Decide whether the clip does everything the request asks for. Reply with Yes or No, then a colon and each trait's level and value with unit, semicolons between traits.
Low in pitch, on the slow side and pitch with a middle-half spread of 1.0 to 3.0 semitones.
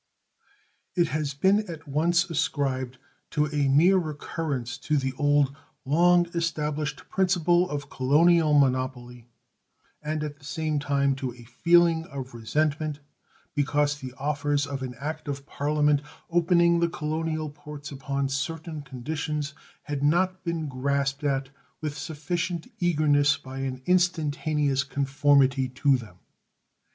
No: medium, 145 Hz; slow, 130 wpm; average, 2.7 semitones